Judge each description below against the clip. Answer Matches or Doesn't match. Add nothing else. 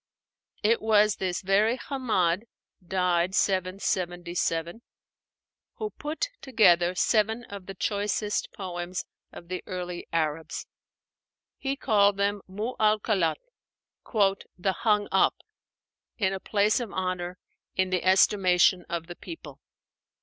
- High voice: Matches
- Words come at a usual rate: Doesn't match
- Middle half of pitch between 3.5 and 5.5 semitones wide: Doesn't match